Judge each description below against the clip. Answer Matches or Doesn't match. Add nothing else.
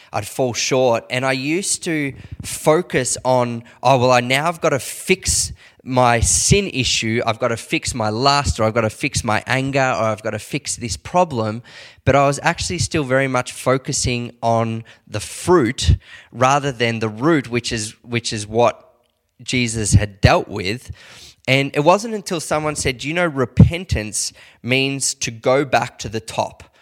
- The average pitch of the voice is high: Doesn't match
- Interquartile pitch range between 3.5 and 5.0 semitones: Matches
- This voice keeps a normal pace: Matches